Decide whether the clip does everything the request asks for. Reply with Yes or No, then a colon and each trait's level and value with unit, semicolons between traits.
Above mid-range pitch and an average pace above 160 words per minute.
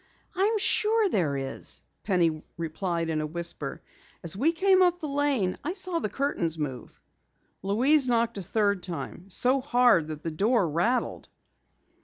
No: high, 205 Hz; average, 155 wpm